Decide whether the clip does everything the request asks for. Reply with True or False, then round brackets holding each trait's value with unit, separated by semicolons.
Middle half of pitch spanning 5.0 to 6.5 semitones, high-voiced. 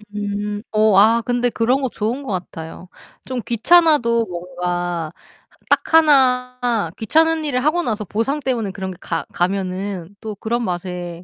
True (5.4 semitones; 220 Hz)